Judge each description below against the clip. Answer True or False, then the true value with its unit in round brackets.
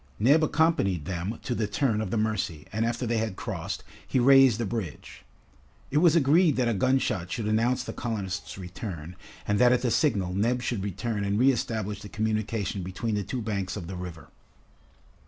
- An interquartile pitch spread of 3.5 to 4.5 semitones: True (4.2 semitones)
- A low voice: True (110 Hz)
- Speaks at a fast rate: False (190 wpm)